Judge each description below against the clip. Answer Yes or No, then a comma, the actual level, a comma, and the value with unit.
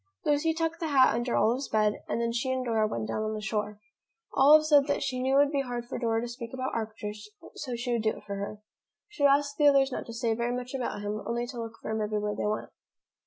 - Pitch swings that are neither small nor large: Yes, average, 4.0 semitones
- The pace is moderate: No, fast, 265 wpm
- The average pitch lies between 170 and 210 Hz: No, high, 240 Hz